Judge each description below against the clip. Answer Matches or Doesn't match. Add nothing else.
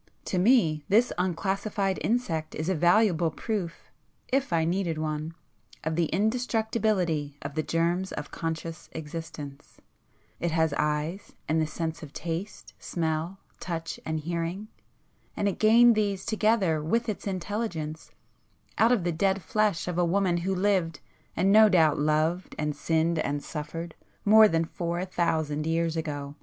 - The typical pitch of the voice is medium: Matches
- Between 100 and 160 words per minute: Matches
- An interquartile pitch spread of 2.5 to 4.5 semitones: Matches